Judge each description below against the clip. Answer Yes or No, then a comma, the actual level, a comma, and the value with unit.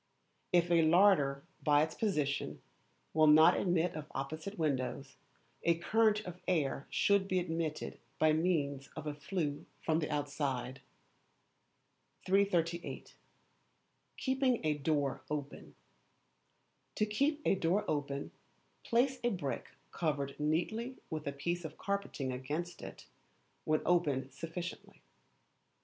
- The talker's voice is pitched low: No, medium, 160 Hz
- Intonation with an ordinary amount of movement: Yes, average, 4.1 semitones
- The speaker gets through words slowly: Yes, slow, 120 wpm